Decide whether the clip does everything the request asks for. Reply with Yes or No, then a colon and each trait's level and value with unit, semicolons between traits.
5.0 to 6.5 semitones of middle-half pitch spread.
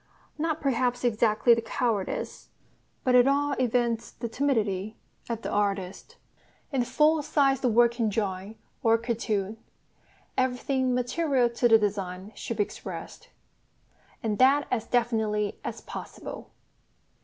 No: average, 3.2 semitones